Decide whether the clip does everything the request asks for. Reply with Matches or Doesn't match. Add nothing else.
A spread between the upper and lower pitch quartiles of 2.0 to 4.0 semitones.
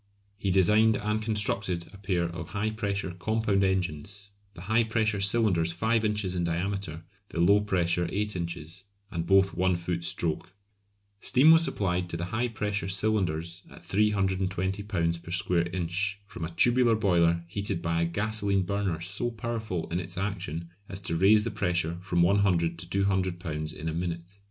Matches